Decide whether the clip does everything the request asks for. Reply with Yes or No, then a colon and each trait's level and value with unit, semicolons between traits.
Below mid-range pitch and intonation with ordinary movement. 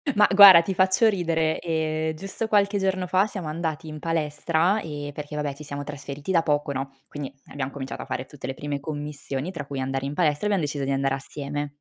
No: medium, 150 Hz; average, 3.5 semitones